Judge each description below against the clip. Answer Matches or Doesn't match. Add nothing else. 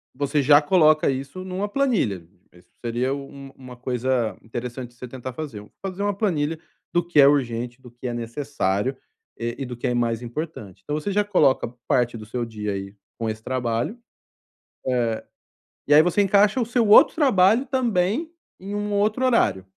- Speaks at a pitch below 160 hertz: Matches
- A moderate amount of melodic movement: Doesn't match